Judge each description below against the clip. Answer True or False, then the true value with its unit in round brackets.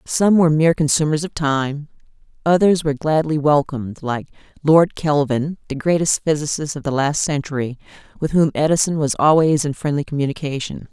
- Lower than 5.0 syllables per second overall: False (5.5 syllables/s)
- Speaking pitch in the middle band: True (150 Hz)